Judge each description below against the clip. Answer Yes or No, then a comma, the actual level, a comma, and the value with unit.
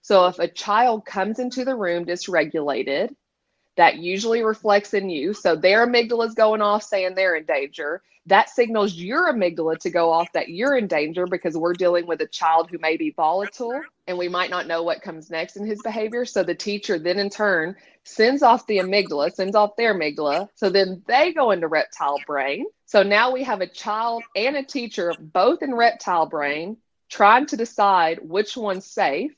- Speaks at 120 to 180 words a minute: No, average, 195 wpm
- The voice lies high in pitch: Yes, high, 195 Hz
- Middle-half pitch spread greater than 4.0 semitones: Yes, average, 4.9 semitones